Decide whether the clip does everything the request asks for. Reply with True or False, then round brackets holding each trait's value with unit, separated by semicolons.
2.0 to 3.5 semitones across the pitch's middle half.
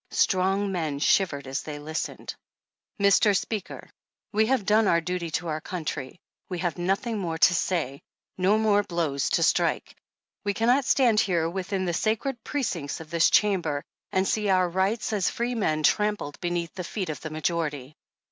False (4.4 semitones)